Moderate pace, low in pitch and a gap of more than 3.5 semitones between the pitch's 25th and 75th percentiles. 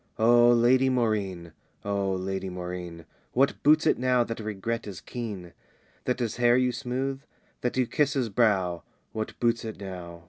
Yes: average, 165 wpm; low, 115 Hz; average, 4.6 semitones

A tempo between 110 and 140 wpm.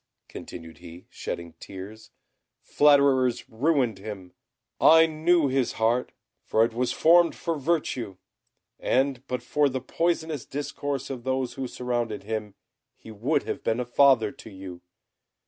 Yes: slow, 135 wpm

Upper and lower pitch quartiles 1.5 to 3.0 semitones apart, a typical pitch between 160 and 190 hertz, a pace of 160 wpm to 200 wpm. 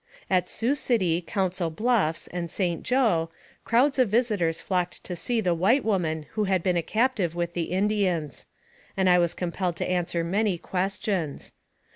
No: average, 3.9 semitones; medium, 185 Hz; average, 165 wpm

